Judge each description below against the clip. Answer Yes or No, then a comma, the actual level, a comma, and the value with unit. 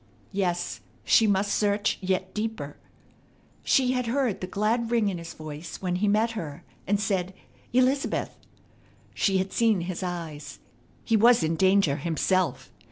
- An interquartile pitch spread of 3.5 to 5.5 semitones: Yes, average, 4.1 semitones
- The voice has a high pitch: Yes, high, 195 Hz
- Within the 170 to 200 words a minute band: No, average, 150 wpm